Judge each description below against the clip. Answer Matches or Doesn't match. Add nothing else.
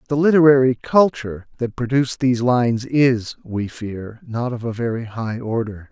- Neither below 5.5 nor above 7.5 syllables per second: Doesn't match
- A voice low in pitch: Matches